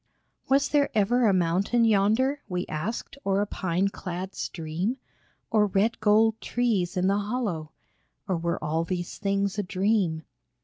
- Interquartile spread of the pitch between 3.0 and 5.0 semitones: Yes, average, 3.8 semitones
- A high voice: Yes, high, 200 Hz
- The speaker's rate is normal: Yes, average, 150 wpm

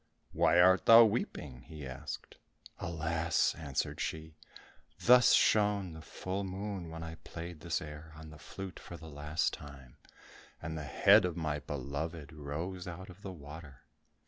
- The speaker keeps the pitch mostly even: No, average, 3.3 semitones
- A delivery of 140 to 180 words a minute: Yes, average, 155 wpm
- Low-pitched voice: Yes, very low, 80 Hz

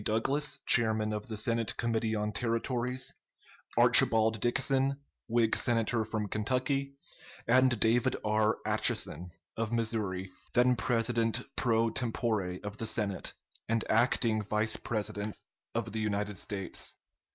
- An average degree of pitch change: No, narrow, 2.1 semitones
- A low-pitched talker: Yes, low, 115 Hz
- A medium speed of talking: No, slow, 120 wpm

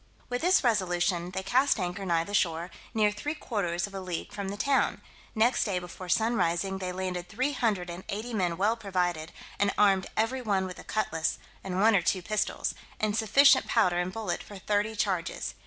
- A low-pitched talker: No, high, 195 Hz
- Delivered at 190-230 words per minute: Yes, average, 200 wpm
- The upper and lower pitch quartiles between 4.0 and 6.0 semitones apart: No, average, 3.6 semitones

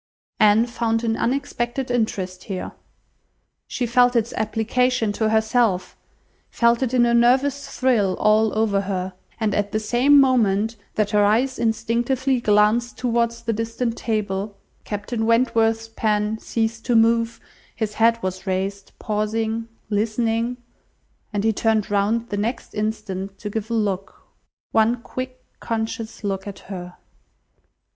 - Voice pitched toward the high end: Yes, high, 225 Hz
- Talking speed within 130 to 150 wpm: Yes, slow, 135 wpm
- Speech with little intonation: Yes, narrow, 2.2 semitones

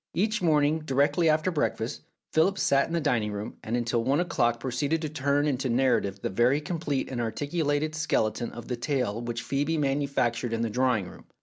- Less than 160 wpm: No, average, 190 wpm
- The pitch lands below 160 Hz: Yes, low, 135 Hz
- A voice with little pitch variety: No, average, 4.5 semitones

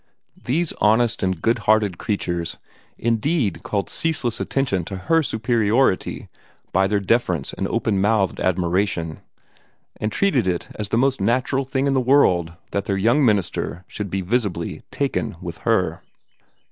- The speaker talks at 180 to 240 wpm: No, average, 145 wpm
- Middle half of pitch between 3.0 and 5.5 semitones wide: Yes, average, 4.7 semitones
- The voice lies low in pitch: Yes, low, 105 Hz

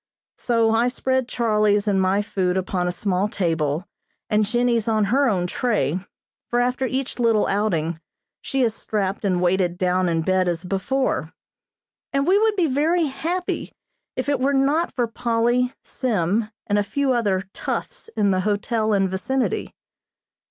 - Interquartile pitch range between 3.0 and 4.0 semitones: No, average, 5.3 semitones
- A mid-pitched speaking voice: No, high, 215 Hz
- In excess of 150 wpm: Yes, average, 160 wpm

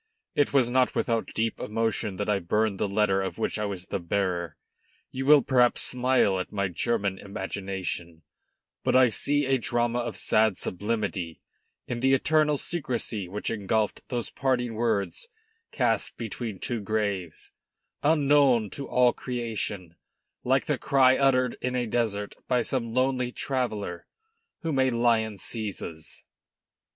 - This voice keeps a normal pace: Yes, average, 145 wpm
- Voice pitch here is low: Yes, low, 115 Hz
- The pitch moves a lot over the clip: No, average, 4.2 semitones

